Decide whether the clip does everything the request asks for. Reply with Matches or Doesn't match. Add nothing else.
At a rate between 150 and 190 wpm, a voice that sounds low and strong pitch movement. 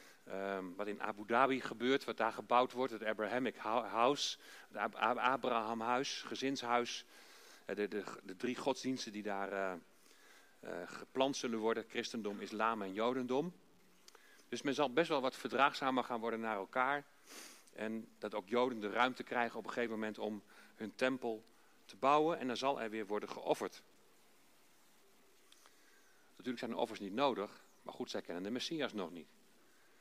Doesn't match